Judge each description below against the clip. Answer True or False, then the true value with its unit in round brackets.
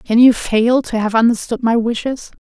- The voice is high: True (235 Hz)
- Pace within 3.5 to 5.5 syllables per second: True (4.8 syllables/s)